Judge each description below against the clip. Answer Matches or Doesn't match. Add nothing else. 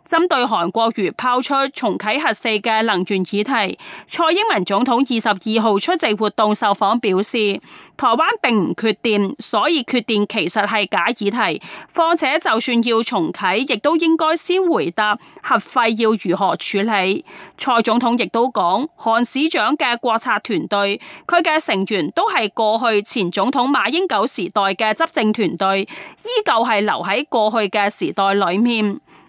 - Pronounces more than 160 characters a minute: Matches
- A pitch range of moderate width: Matches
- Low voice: Doesn't match